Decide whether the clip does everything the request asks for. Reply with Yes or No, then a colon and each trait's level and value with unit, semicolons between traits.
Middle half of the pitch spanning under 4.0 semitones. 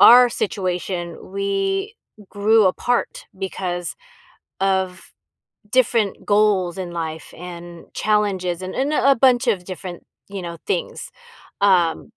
No: average, 4.8 semitones